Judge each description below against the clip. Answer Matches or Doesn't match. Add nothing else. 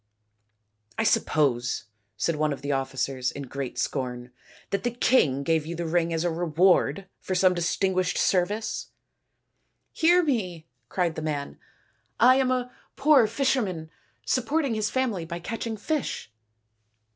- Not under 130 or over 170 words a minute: Matches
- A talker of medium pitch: Matches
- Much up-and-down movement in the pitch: Matches